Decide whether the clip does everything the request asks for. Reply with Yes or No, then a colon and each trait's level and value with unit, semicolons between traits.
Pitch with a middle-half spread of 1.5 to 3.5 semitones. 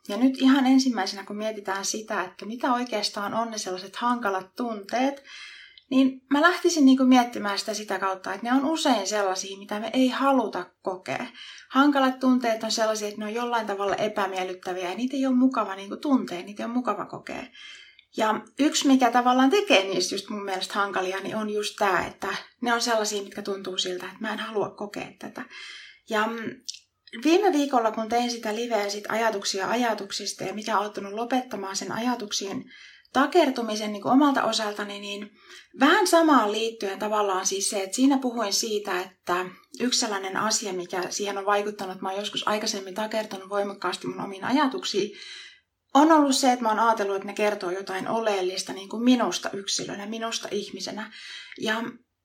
No: average, 4.3 semitones